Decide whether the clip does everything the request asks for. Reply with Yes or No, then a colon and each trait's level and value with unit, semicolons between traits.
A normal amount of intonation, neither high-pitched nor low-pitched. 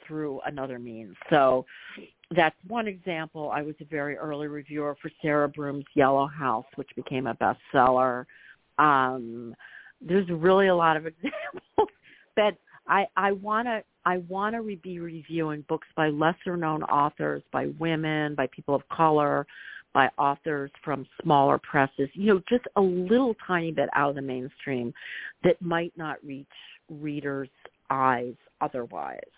Yes: average, 4.1 semitones; medium, 150 Hz